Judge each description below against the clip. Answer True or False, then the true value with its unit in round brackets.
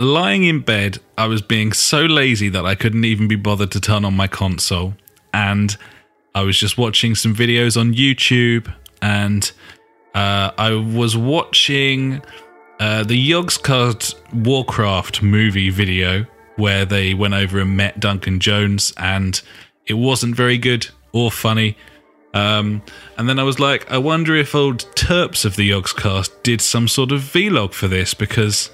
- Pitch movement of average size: True (3.5 semitones)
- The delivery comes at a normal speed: True (160 wpm)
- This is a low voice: True (110 Hz)